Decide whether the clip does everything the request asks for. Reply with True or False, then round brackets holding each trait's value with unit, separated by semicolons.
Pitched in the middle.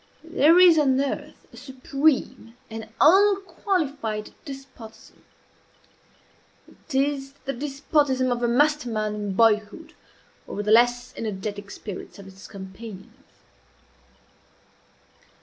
False (255 Hz)